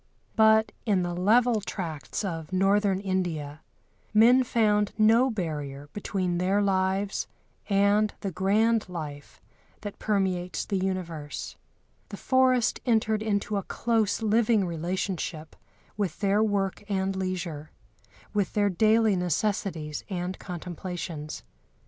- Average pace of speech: No, slow, 115 wpm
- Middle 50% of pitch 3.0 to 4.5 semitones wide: Yes, average, 3.3 semitones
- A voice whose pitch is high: Yes, high, 195 Hz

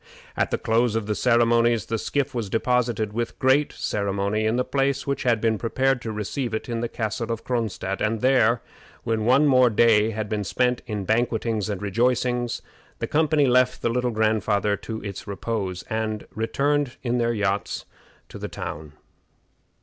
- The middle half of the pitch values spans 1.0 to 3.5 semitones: Yes, narrow, 2.6 semitones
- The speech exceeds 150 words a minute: Yes, average, 175 wpm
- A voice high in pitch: No, low, 115 Hz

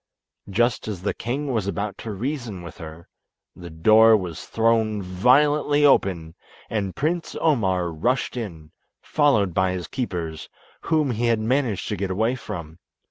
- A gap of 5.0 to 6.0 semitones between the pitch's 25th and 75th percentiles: Yes, wide, 5.6 semitones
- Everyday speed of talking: Yes, average, 150 wpm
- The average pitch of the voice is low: Yes, low, 105 Hz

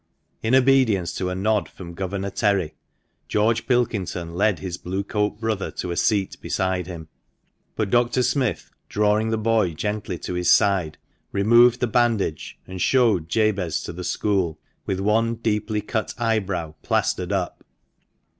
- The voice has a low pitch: Yes, low, 105 Hz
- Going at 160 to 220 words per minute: No, average, 150 wpm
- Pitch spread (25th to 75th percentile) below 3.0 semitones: No, average, 3.5 semitones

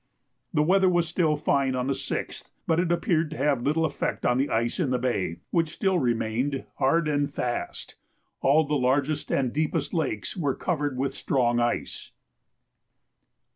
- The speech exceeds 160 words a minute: Yes, average, 170 wpm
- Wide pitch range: No, average, 4.0 semitones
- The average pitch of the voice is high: No, medium, 145 Hz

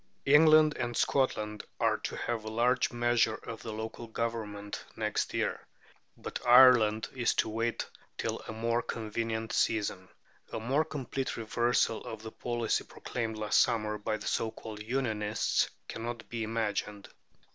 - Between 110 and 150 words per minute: Yes, average, 145 wpm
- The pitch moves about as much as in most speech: No, narrow, 1.8 semitones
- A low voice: Yes, low, 115 Hz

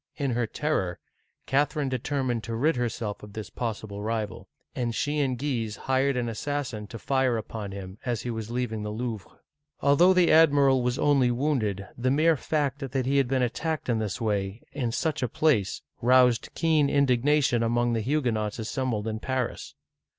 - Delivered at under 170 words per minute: No, average, 180 wpm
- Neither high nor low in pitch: No, low, 125 Hz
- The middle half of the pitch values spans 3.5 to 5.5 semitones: Yes, average, 4.0 semitones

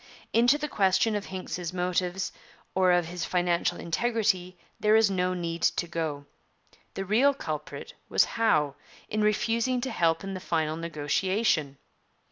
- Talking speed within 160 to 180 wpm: No, average, 145 wpm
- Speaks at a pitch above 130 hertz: Yes, medium, 185 Hz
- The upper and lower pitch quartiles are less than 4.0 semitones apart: No, average, 4.3 semitones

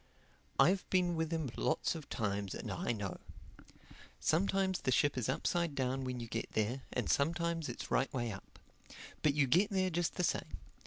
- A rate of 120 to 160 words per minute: No, average, 180 wpm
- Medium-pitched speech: Yes, medium, 145 Hz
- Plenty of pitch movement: Yes, wide, 5.7 semitones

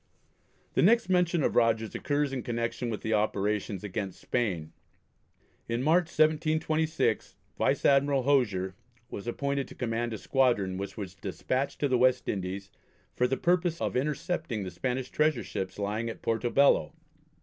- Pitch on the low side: Yes, low, 125 Hz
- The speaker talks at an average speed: Yes, average, 155 wpm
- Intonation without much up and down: No, wide, 5.6 semitones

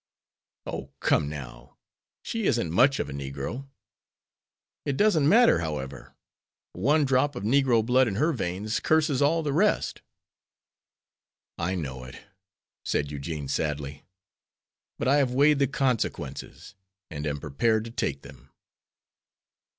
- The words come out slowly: Yes, slow, 130 wpm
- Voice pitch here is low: Yes, low, 115 Hz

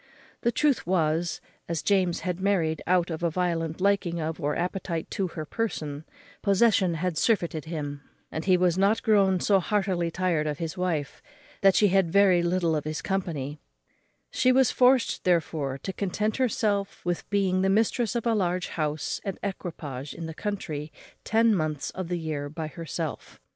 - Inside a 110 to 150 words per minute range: No, average, 175 wpm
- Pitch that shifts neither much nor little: Yes, average, 3.8 semitones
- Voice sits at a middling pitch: Yes, medium, 180 Hz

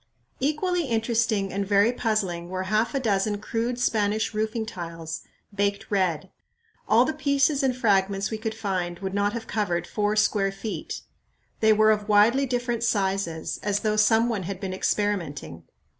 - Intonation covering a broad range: No, average, 2.8 semitones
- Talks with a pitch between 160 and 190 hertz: No, high, 210 Hz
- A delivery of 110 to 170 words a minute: Yes, average, 160 wpm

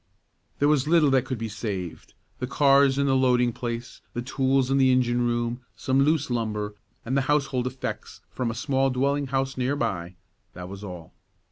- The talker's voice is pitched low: Yes, low, 130 Hz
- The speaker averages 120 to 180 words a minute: No, average, 190 wpm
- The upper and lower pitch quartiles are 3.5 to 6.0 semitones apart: No, narrow, 2.6 semitones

